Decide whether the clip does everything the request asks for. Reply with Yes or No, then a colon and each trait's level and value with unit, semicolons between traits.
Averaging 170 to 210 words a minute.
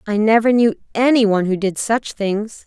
Yes: fast, 205 wpm